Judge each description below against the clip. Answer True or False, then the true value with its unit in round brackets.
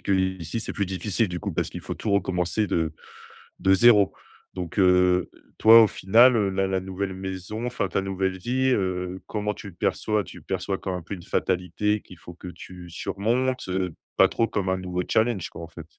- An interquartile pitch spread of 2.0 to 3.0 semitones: True (2.5 semitones)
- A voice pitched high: False (95 Hz)